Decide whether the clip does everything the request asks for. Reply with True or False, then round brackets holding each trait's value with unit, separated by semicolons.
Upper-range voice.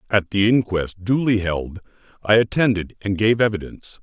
False (100 Hz)